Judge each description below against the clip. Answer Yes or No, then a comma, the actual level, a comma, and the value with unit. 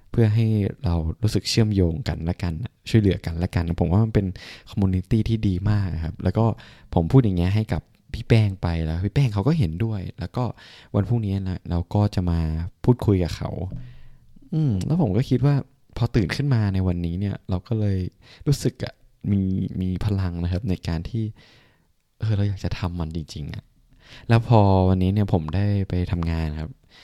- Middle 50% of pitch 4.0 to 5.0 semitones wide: Yes, average, 4.4 semitones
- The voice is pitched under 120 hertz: Yes, low, 100 Hz